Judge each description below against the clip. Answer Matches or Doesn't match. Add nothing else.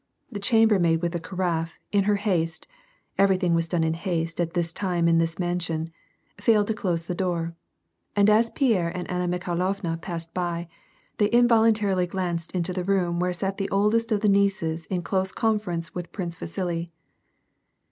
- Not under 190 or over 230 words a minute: Doesn't match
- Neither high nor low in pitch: Matches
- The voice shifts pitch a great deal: Doesn't match